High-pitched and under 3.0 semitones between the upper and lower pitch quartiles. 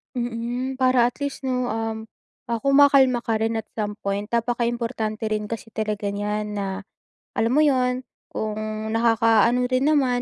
Yes: high, 230 Hz; narrow, 2.6 semitones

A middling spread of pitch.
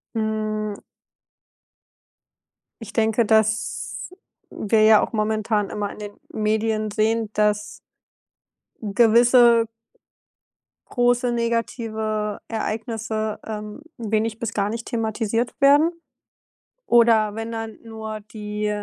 No: narrow, 1.3 semitones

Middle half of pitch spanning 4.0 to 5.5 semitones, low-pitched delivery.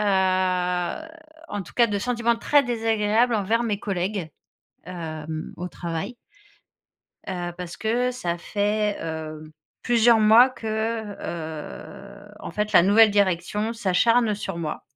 No: average, 4.4 semitones; high, 205 Hz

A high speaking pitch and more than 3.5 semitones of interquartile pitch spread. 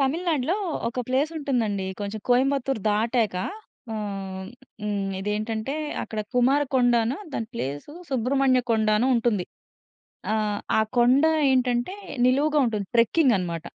Yes: high, 235 Hz; average, 4.1 semitones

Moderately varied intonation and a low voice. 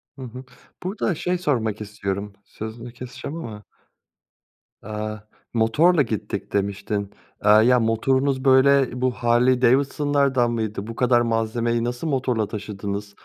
Yes: average, 3.5 semitones; low, 120 Hz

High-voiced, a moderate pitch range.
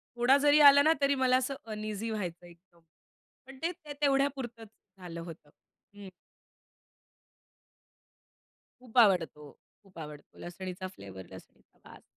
No: high, 215 Hz; wide, 7.8 semitones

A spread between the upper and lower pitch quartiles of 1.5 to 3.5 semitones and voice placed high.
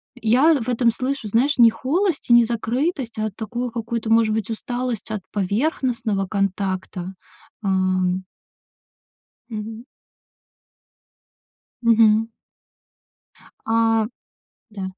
Yes: average, 2.9 semitones; high, 225 Hz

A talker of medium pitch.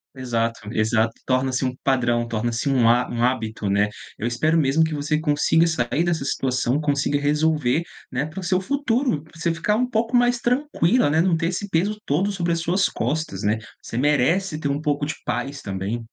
Yes: medium, 145 Hz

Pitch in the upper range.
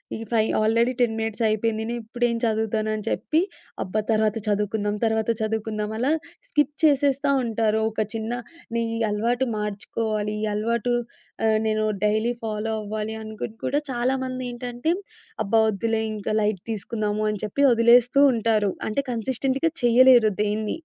Yes: high, 220 Hz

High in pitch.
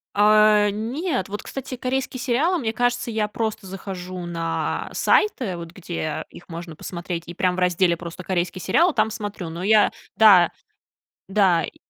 Yes: high, 200 Hz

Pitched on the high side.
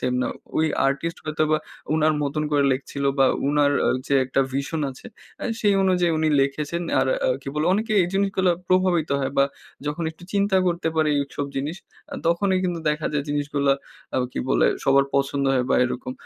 No: medium, 155 Hz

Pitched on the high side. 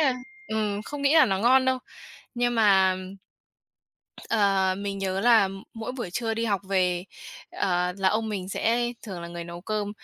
Yes: high, 205 Hz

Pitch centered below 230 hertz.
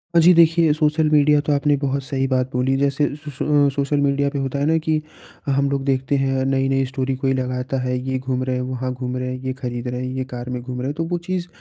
Yes: low, 135 Hz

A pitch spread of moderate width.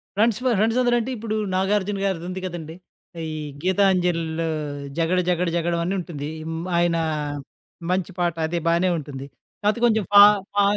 Yes: average, 3.4 semitones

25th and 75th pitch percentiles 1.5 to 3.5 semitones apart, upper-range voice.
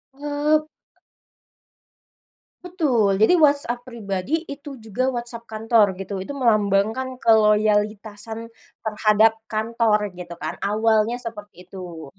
Yes: average, 2.8 semitones; high, 220 Hz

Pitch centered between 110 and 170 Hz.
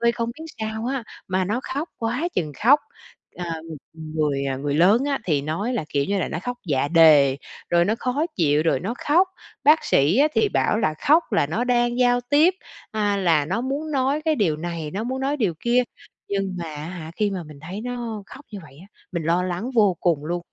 No: high, 200 Hz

